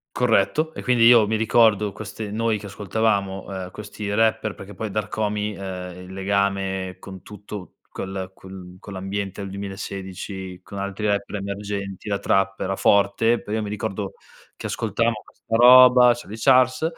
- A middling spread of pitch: No, narrow, 2.3 semitones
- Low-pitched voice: Yes, low, 100 Hz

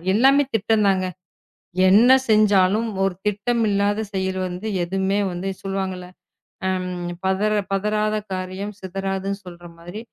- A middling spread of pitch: No, narrow, 2.1 semitones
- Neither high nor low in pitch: No, high, 195 Hz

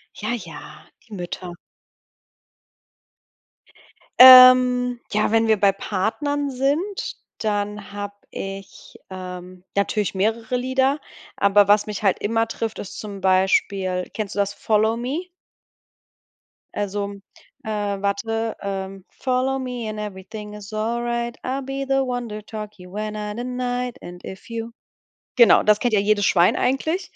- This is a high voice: Yes, high, 215 Hz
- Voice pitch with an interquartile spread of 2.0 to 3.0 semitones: No, average, 3.7 semitones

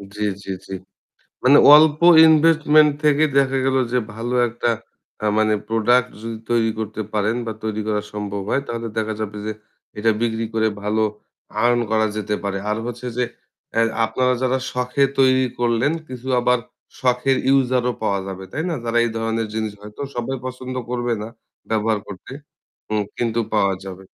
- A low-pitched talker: Yes, low, 115 Hz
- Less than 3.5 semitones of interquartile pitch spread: Yes, average, 2.8 semitones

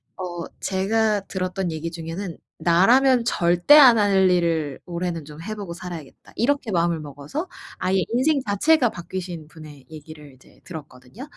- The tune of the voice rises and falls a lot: No, average, 4.7 semitones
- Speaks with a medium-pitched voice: Yes, medium, 180 Hz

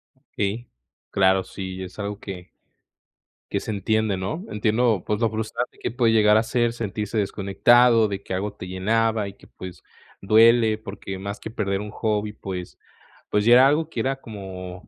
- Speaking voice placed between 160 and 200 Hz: No, low, 105 Hz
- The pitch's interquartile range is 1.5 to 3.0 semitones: Yes, average, 2.7 semitones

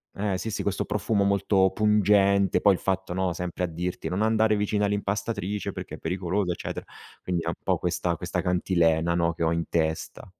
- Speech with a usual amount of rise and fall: Yes, average, 3.0 semitones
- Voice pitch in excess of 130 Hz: No, very low, 95 Hz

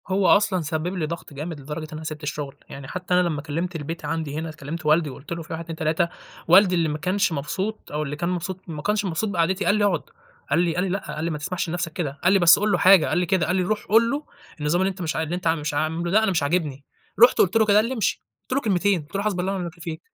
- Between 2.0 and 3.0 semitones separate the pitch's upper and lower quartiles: No, average, 3.4 semitones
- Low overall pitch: No, medium, 170 Hz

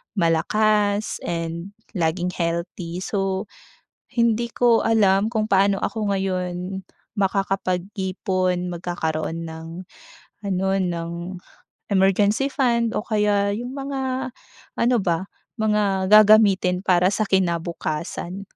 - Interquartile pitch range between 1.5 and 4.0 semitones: Yes, average, 3.2 semitones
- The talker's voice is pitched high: Yes, high, 195 Hz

